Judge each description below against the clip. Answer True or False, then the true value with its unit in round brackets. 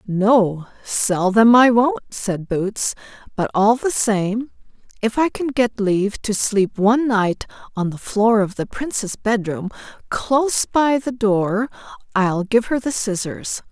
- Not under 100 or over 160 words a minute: True (155 wpm)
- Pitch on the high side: True (220 Hz)